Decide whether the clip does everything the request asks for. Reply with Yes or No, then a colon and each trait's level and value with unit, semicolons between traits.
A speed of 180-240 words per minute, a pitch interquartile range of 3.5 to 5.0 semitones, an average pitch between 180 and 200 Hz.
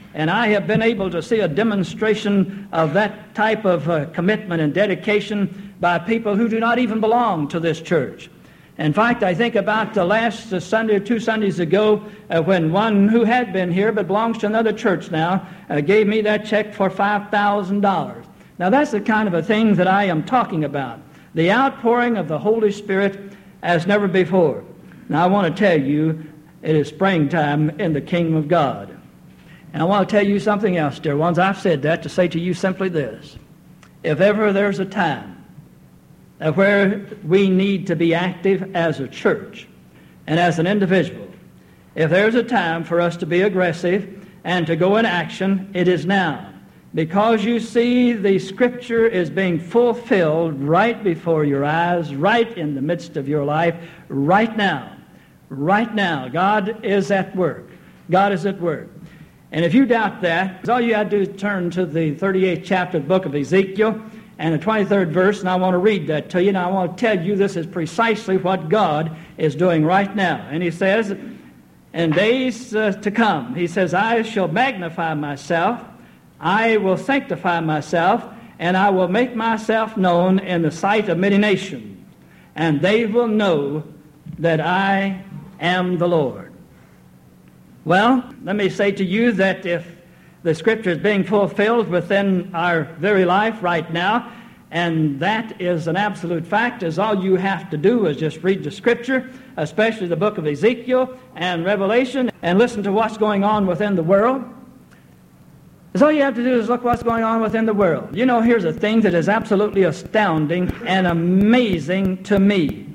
Yes: average, 185 wpm; average, 4.0 semitones; high, 190 Hz